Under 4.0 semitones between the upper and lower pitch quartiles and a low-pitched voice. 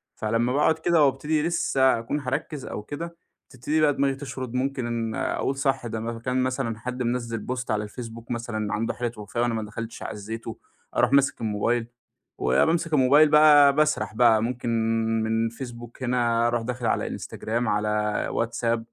Yes: average, 2.9 semitones; low, 120 Hz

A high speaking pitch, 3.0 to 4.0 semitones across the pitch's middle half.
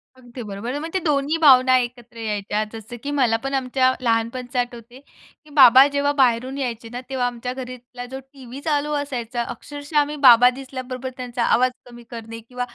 No: very high, 255 Hz; narrow, 2.4 semitones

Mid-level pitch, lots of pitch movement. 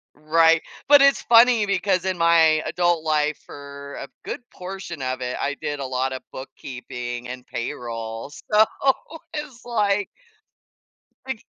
Yes: medium, 155 Hz; wide, 7.1 semitones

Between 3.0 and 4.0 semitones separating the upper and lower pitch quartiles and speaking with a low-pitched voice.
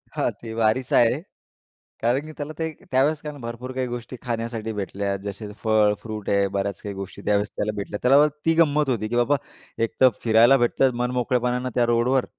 Yes: average, 3.4 semitones; low, 120 Hz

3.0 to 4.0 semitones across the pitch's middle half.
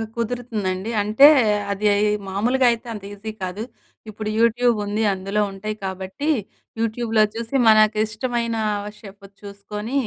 No: narrow, 2.5 semitones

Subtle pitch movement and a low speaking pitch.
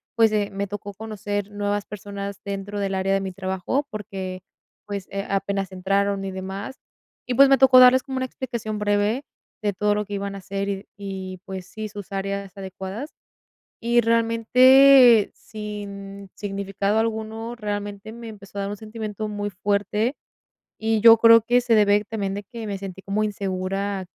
No: narrow, 2.0 semitones; high, 205 Hz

